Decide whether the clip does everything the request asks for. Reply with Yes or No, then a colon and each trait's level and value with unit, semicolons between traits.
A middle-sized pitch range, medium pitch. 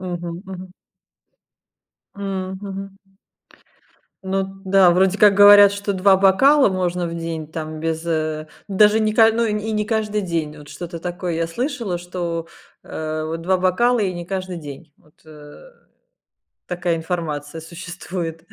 Yes: average, 3.2 semitones; medium, 180 Hz